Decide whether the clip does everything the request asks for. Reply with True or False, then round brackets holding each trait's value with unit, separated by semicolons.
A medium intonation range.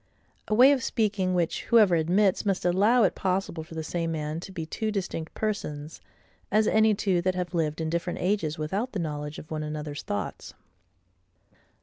True (4.5 semitones)